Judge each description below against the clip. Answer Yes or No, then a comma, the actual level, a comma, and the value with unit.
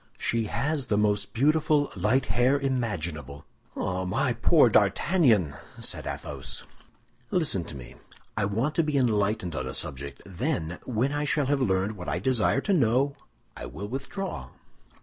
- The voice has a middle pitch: No, low, 115 Hz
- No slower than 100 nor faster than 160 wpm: Yes, average, 155 wpm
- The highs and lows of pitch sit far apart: Yes, wide, 6.9 semitones